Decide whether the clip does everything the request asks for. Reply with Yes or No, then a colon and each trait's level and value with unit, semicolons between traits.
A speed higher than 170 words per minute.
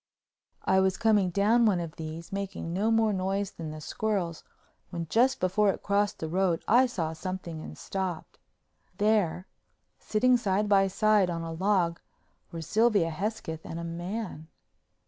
No: average, 160 wpm